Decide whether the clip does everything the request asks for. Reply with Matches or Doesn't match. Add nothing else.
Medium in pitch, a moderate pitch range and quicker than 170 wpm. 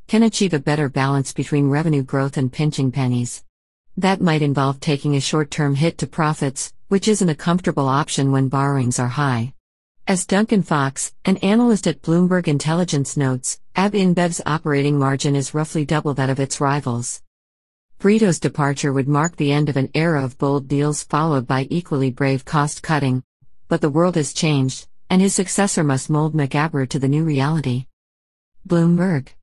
Doesn't match